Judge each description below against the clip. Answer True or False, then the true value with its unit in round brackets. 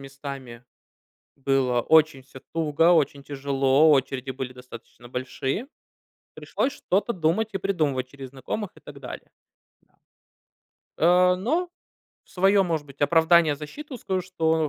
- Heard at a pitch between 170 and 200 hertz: False (150 Hz)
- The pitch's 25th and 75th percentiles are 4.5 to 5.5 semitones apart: True (5.0 semitones)